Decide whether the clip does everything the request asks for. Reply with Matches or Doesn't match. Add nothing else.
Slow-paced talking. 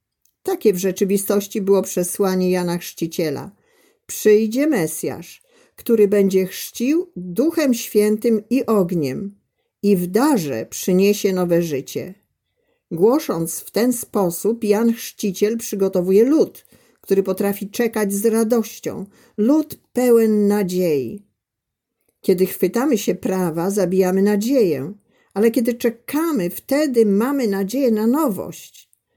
Matches